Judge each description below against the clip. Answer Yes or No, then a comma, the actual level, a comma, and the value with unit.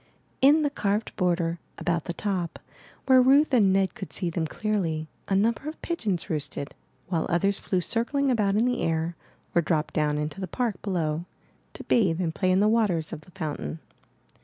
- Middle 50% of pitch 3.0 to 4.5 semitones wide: No, average, 5.1 semitones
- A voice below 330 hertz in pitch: Yes, medium, 185 Hz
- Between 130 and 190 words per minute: No, fast, 205 wpm